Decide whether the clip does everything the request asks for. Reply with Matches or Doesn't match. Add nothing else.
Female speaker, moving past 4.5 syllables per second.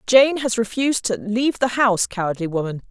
Matches